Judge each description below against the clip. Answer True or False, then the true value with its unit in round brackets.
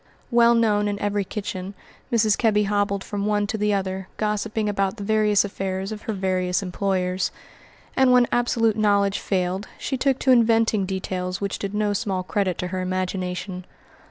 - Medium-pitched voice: False (200 Hz)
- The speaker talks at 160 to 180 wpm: True (170 wpm)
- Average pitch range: False (2.2 semitones)